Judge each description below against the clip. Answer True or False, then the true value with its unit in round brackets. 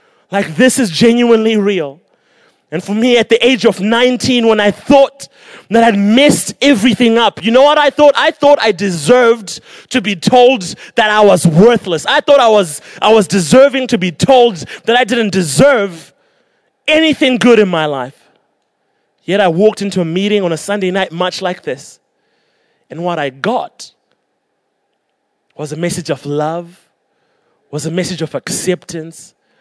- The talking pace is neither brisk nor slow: True (170 wpm)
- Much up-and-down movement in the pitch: True (5.7 semitones)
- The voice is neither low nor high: False (215 Hz)